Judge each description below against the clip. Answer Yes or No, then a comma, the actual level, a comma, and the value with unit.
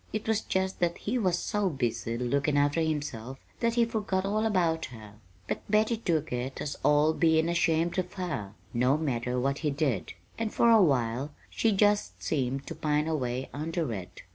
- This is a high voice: No, medium, 155 Hz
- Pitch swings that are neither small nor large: No, wide, 6.4 semitones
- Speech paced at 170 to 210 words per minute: Yes, average, 185 wpm